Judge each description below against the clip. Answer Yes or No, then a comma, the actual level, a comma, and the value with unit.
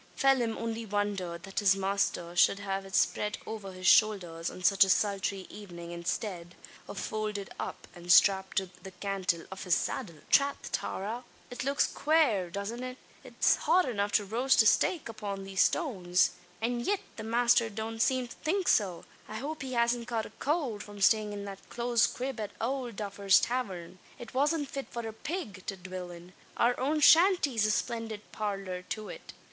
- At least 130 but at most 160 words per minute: No, average, 185 wpm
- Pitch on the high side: Yes, high, 210 Hz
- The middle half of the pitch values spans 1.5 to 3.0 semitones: No, average, 4.1 semitones